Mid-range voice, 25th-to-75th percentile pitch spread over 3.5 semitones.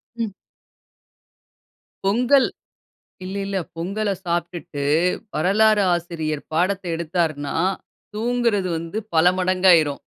Yes: medium, 180 Hz; average, 4.1 semitones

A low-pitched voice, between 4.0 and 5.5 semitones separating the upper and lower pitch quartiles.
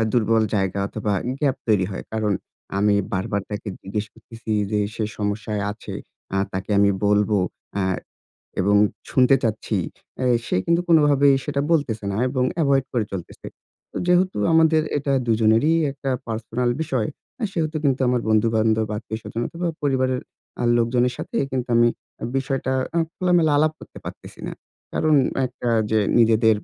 Yes: low, 115 Hz; average, 4.6 semitones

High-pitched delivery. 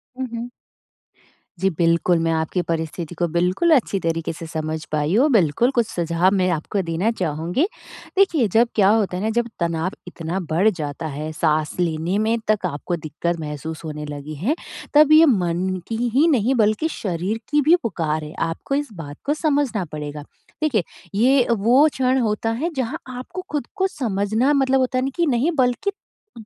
Yes: high, 195 Hz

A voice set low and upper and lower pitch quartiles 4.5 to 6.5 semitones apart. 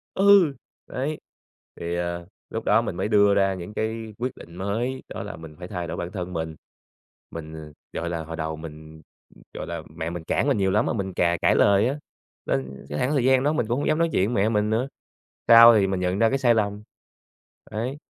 Yes: low, 100 Hz; wide, 5.5 semitones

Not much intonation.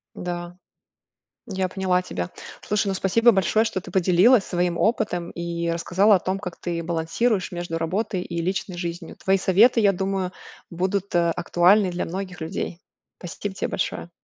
Yes: narrow, 2.2 semitones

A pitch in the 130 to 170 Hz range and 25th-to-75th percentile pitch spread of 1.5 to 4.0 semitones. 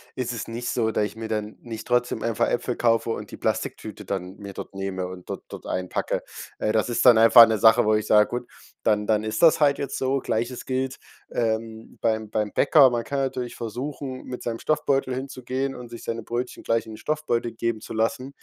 No: low, 115 Hz; average, 2.7 semitones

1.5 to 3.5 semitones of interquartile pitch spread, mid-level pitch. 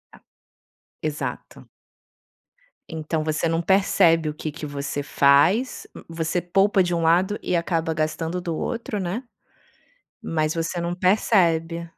Yes: narrow, 2.4 semitones; medium, 165 Hz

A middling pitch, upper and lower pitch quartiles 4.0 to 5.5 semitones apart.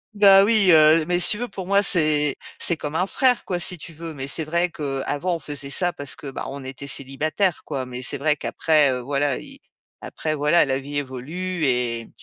Yes: medium, 155 Hz; average, 4.3 semitones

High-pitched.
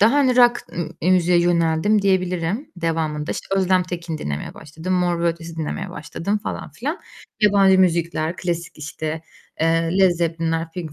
No: medium, 170 Hz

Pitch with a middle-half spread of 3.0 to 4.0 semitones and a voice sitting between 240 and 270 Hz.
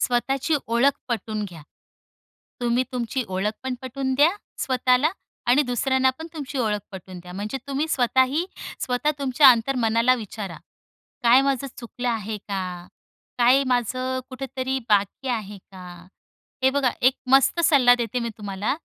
Yes: average, 3.6 semitones; very high, 250 Hz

